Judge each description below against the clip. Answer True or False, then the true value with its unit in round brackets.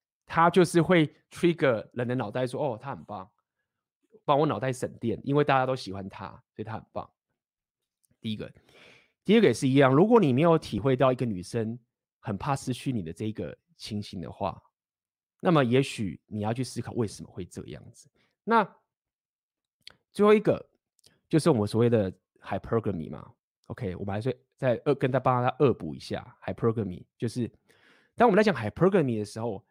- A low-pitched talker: True (125 Hz)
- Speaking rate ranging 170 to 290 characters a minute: False (315 characters per minute)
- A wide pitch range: True (5.7 semitones)